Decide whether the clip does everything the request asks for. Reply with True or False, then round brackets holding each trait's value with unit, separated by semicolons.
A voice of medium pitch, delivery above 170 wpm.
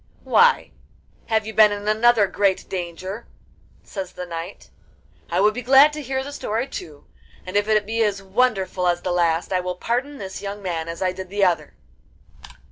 False (200 Hz; 190 wpm)